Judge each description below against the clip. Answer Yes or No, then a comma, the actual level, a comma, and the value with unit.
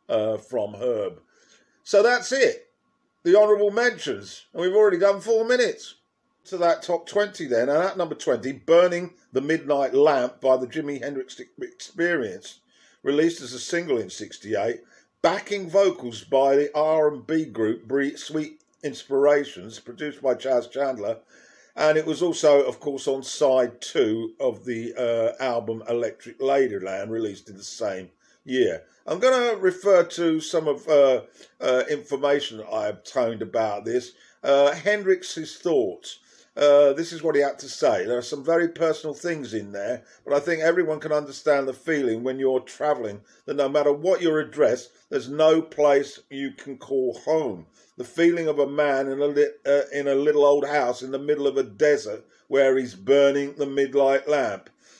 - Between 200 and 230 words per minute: No, average, 170 wpm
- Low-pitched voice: No, medium, 145 Hz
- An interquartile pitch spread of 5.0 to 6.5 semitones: No, average, 4.3 semitones